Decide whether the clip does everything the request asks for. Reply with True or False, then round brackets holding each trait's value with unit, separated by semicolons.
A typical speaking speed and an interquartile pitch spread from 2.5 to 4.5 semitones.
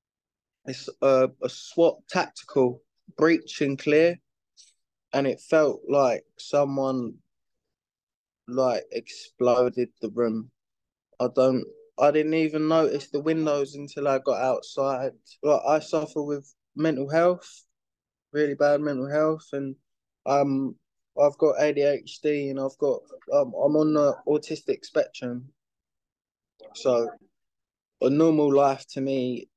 False (120 wpm; 2.8 semitones)